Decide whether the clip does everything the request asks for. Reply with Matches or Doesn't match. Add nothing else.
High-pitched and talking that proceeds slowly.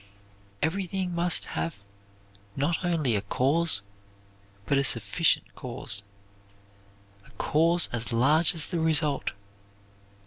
Doesn't match